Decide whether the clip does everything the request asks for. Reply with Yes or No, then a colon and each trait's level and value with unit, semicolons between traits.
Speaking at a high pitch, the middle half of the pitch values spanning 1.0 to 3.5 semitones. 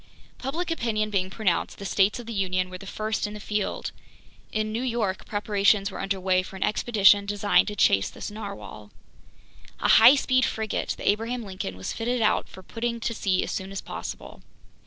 Yes: high, 210 Hz; average, 2.9 semitones